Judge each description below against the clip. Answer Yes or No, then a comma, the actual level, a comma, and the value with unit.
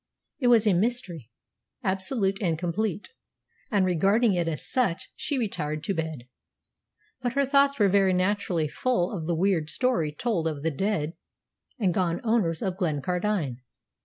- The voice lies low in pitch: No, high, 190 Hz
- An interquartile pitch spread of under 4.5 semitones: No, average, 5.0 semitones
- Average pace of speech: Yes, average, 155 wpm